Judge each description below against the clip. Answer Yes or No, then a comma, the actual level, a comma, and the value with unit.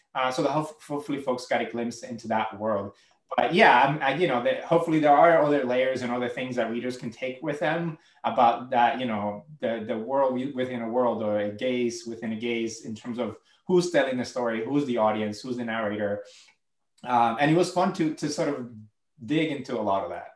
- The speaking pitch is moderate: No, low, 125 Hz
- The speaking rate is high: Yes, fast, 220 wpm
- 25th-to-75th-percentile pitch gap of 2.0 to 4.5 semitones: Yes, average, 4.2 semitones